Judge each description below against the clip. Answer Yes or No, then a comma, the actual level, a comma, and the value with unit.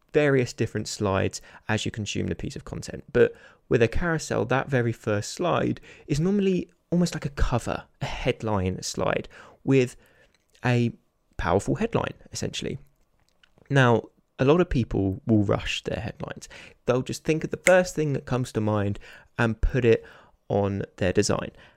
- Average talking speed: Yes, average, 160 wpm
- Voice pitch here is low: Yes, low, 120 Hz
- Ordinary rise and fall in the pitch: No, wide, 6.1 semitones